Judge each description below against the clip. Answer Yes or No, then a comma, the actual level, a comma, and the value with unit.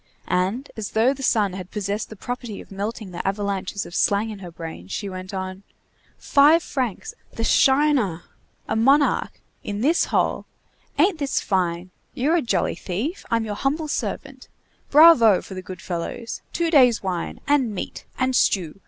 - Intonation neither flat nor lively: No, wide, 6.3 semitones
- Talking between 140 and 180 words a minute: Yes, average, 170 wpm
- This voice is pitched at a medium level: No, high, 215 Hz